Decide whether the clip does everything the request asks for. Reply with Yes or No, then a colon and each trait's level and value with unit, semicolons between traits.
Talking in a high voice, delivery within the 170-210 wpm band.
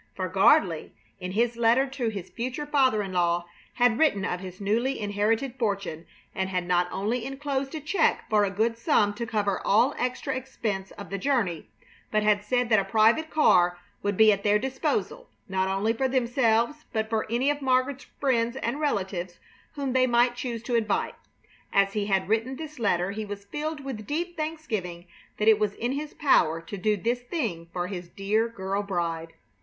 Yes: high, 220 Hz; average, 190 wpm